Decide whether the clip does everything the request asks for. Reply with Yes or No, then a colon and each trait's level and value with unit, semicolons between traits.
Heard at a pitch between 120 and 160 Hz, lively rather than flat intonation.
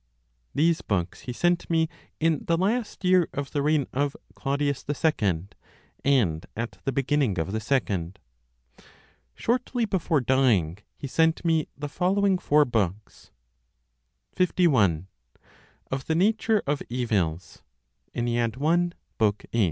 Yes: medium, 140 Hz; wide, 7.0 semitones